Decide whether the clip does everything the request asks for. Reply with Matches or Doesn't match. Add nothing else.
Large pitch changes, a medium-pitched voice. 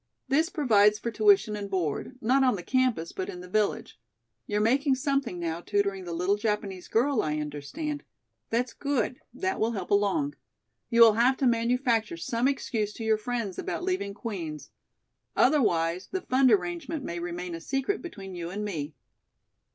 Doesn't match